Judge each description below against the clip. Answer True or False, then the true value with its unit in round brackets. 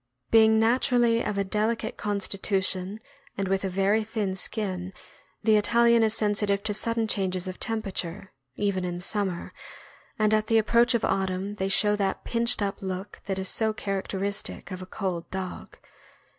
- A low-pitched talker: False (200 Hz)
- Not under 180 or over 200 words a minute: False (170 wpm)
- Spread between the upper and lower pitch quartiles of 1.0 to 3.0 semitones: True (2.5 semitones)